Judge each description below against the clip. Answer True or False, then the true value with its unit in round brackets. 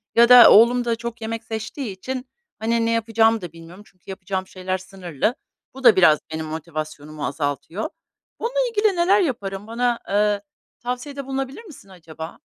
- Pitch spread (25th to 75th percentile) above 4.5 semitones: True (5.2 semitones)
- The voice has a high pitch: True (220 Hz)